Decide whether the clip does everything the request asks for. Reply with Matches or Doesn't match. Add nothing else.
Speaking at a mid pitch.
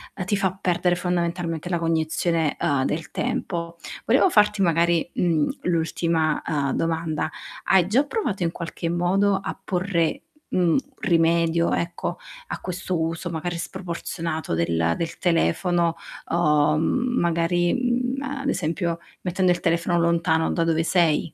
Matches